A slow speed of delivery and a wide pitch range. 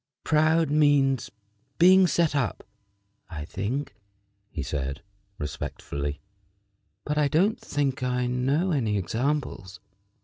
Yes: slow, 105 wpm; wide, 7.1 semitones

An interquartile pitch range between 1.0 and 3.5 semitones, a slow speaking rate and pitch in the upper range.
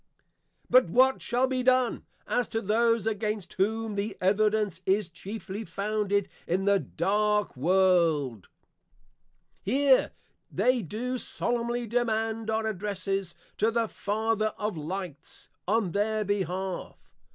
Yes: average, 2.9 semitones; slow, 120 wpm; high, 210 Hz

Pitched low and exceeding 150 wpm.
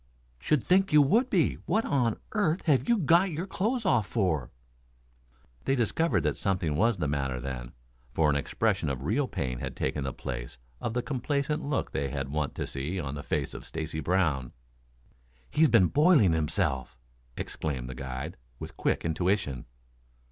Yes: very low, 95 Hz; average, 170 wpm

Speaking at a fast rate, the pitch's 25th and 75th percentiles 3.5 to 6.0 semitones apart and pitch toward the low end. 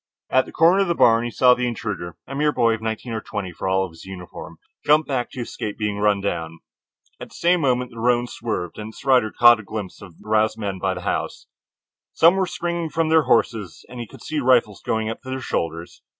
Yes: fast, 240 wpm; average, 4.3 semitones; low, 115 Hz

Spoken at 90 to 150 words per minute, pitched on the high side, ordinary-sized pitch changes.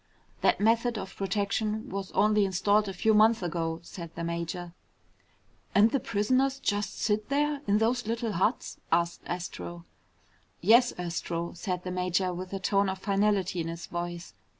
No: average, 160 wpm; high, 195 Hz; average, 3.7 semitones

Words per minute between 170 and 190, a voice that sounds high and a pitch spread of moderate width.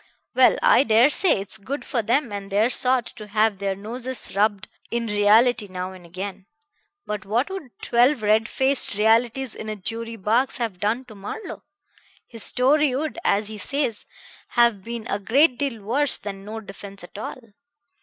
Yes: average, 175 wpm; high, 220 Hz; average, 3.7 semitones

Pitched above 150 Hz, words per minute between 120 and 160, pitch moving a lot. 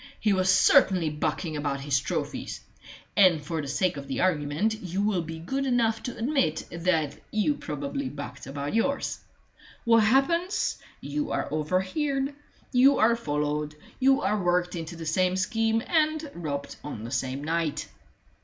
Yes: medium, 185 Hz; average, 155 wpm; wide, 7.5 semitones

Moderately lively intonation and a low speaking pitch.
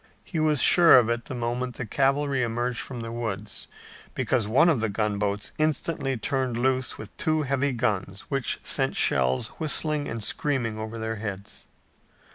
Yes: average, 3.9 semitones; low, 120 Hz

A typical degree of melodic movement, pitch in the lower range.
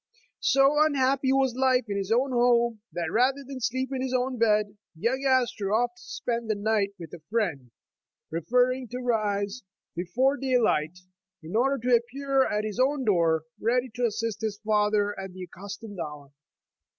No: average, 4.2 semitones; high, 230 Hz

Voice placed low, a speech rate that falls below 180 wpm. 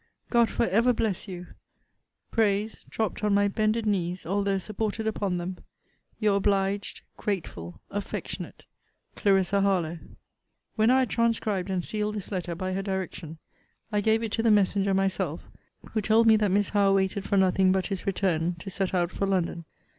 No: high, 195 Hz; average, 170 wpm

